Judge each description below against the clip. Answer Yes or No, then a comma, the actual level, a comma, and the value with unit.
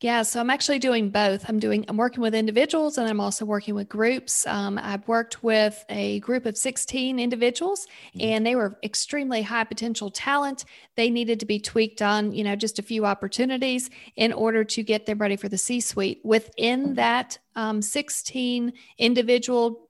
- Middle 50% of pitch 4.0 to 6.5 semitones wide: No, average, 2.7 semitones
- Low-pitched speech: No, high, 230 Hz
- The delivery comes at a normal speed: Yes, average, 185 wpm